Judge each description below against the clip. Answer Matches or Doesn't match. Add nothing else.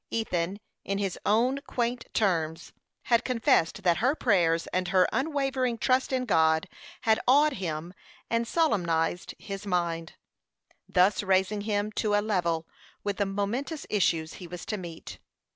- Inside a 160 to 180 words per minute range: Doesn't match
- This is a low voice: Doesn't match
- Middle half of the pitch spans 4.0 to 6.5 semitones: Matches